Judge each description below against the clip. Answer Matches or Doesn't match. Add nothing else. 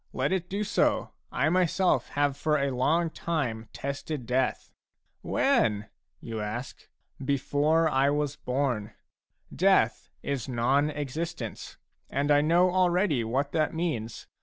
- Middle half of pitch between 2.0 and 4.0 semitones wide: Doesn't match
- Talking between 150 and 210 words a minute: Doesn't match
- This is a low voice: Doesn't match